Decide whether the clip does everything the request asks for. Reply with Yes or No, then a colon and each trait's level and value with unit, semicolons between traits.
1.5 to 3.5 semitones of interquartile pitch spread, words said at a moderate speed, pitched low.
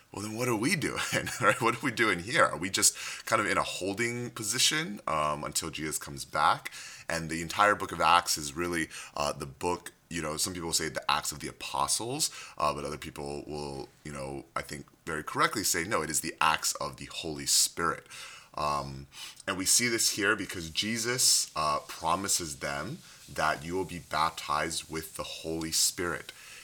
No: average, 4.6 semitones; average, 195 wpm; very low, 80 Hz